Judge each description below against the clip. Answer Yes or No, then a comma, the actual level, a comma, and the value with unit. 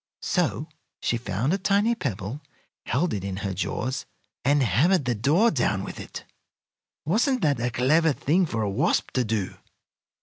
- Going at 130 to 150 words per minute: No, average, 165 wpm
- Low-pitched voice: Yes, low, 130 Hz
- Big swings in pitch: Yes, wide, 7.5 semitones